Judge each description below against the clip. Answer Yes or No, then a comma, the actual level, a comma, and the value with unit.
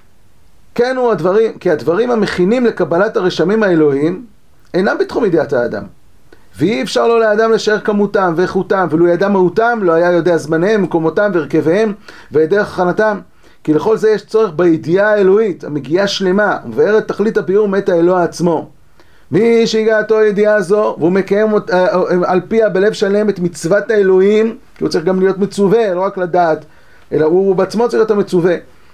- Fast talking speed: Yes, fast, 155 wpm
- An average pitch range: Yes, average, 3.4 semitones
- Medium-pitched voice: No, high, 200 Hz